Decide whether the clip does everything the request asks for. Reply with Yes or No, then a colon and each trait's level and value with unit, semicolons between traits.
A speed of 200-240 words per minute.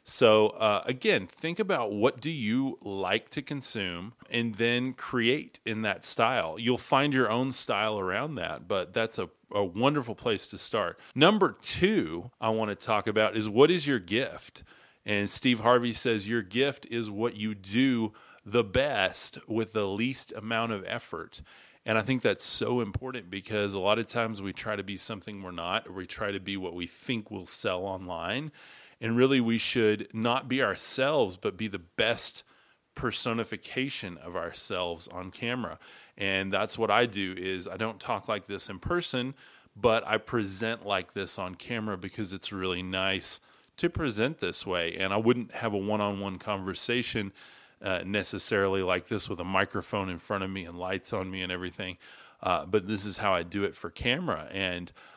No: average, 185 wpm